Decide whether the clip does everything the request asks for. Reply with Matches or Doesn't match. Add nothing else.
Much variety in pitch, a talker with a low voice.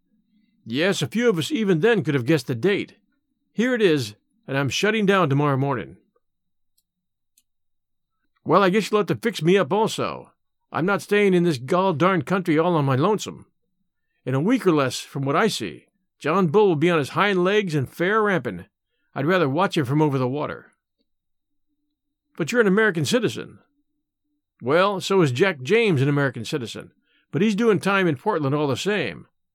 Doesn't match